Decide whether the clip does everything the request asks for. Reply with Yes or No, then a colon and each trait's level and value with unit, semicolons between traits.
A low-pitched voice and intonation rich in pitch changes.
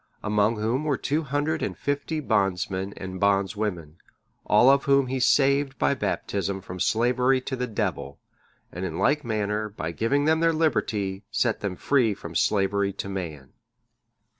Yes: low, 110 Hz; wide, 6.1 semitones